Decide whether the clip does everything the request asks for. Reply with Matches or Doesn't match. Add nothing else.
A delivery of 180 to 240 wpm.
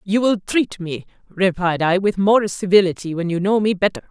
Matches